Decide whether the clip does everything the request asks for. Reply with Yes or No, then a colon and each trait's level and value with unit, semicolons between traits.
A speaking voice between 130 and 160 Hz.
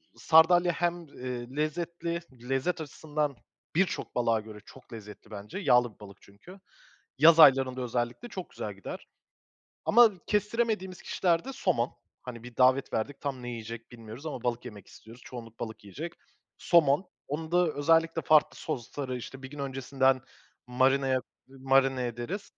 Yes: low, 135 Hz